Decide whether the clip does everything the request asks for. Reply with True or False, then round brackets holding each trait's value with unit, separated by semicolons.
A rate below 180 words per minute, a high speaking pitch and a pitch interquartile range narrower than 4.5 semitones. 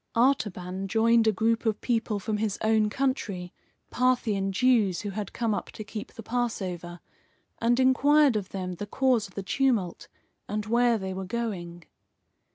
True (165 wpm; 215 Hz; 3.7 semitones)